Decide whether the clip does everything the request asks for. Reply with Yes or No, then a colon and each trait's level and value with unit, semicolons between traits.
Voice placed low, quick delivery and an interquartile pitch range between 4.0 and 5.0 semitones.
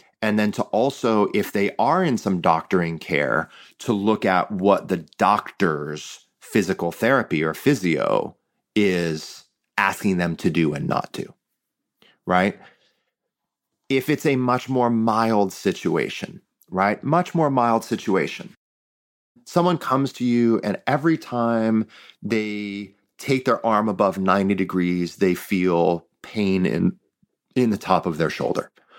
No: low, 110 Hz; slow, 135 wpm; average, 4.7 semitones